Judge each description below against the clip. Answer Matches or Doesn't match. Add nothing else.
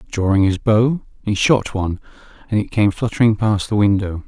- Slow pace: Doesn't match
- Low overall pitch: Matches